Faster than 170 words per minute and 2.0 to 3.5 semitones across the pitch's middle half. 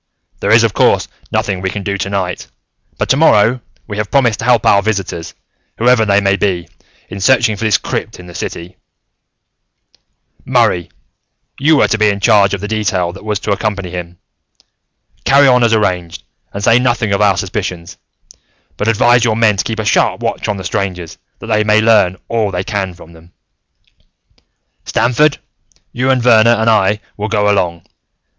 Yes: average, 180 wpm; average, 3.1 semitones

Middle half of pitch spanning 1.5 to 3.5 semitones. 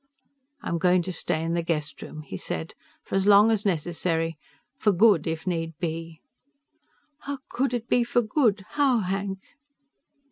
No: average, 4.6 semitones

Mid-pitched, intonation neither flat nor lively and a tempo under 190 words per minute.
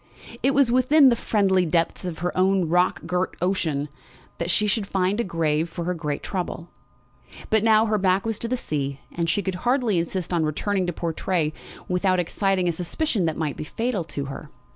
No: medium, 180 Hz; average, 3.9 semitones; average, 200 wpm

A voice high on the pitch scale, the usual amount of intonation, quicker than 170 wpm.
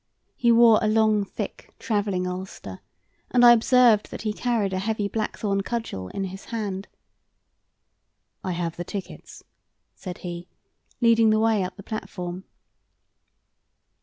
No: high, 205 Hz; average, 3.2 semitones; slow, 135 wpm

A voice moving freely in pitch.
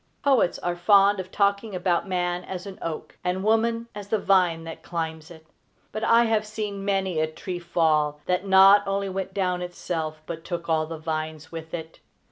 No: average, 3.5 semitones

